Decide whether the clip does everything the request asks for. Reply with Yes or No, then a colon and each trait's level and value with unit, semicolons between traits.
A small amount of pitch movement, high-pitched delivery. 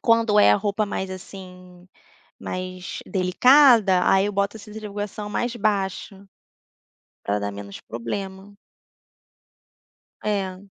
Yes: narrow, 2.3 semitones; high, 195 Hz